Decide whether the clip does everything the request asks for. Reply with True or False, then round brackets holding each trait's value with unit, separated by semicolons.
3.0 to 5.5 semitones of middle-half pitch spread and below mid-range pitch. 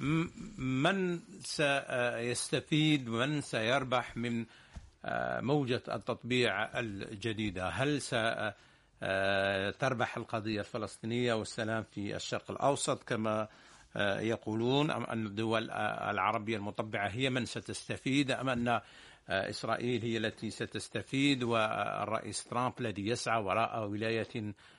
False (2.6 semitones; 115 Hz)